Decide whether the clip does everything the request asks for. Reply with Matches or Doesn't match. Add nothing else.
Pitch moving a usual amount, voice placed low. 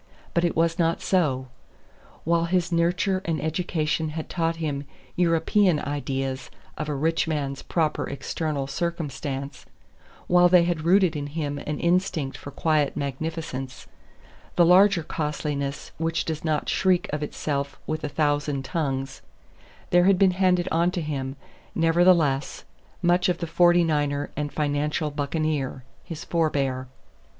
Doesn't match